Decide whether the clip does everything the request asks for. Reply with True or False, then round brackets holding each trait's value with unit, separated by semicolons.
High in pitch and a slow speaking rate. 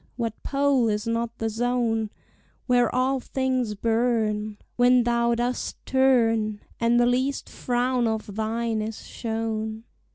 True (235 Hz; 130 wpm)